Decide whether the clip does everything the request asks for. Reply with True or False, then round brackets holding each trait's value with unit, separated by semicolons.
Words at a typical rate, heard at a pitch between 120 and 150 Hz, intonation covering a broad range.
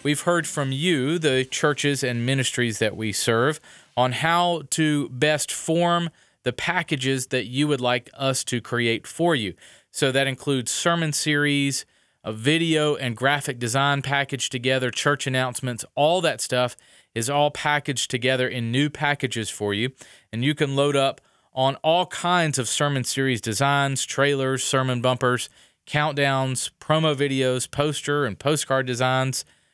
False (150 wpm; 135 Hz; 2.7 semitones)